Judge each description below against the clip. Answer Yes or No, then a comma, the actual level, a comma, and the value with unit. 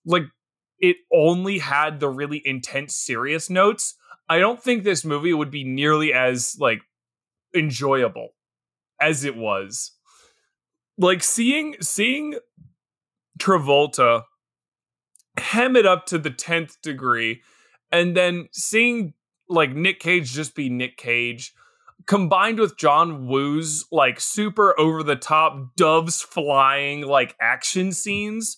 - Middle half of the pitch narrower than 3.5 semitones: No, wide, 5.4 semitones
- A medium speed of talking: No, slow, 120 wpm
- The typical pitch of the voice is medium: Yes, medium, 160 Hz